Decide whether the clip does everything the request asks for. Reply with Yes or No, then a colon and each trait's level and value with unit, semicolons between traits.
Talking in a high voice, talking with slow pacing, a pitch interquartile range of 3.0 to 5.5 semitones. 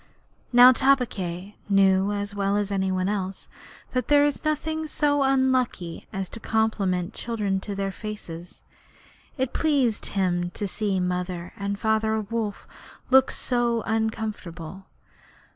Yes: high, 205 Hz; slow, 130 wpm; average, 4.2 semitones